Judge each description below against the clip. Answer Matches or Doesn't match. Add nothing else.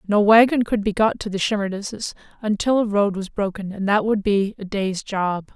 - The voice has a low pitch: Doesn't match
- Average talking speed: Doesn't match